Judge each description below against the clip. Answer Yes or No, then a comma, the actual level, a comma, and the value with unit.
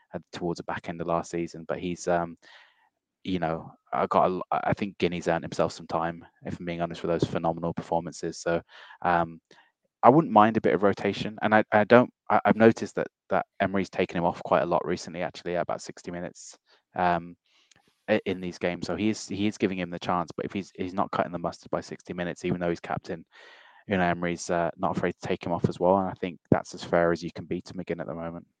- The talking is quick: Yes, fast, 240 wpm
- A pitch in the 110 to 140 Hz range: No, very low, 85 Hz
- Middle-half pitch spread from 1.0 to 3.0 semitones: Yes, narrow, 2.5 semitones